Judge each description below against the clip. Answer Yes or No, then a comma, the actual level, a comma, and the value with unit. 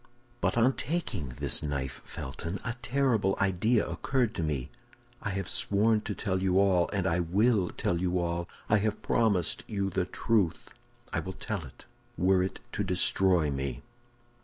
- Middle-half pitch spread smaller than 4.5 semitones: Yes, average, 3.8 semitones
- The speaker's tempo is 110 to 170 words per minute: Yes, average, 165 wpm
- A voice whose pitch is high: No, very low, 95 Hz